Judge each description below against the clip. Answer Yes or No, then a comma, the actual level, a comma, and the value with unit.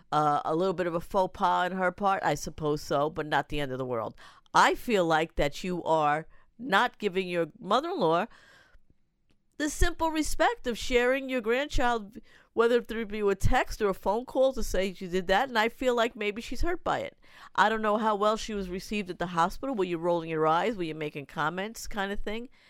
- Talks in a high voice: Yes, high, 195 Hz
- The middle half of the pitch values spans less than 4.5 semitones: No, average, 5.2 semitones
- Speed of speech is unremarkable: No, fast, 225 wpm